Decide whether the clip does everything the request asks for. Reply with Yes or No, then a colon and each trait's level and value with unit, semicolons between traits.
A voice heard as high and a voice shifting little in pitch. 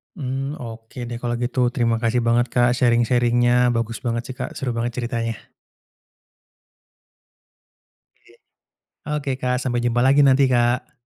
No: low, 120 Hz; narrow, 1.2 semitones